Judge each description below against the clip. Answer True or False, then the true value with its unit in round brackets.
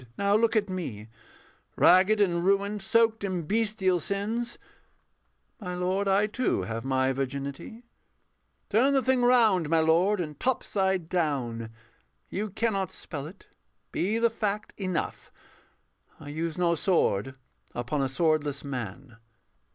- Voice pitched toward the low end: False (185 Hz)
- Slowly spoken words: True (130 wpm)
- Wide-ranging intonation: True (6.2 semitones)